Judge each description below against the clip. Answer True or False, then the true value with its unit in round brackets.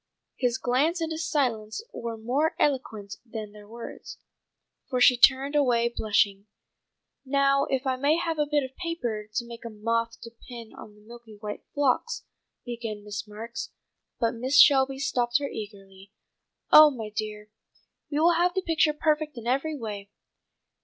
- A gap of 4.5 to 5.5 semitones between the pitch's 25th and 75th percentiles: True (4.9 semitones)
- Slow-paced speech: False (165 wpm)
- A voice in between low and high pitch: False (245 Hz)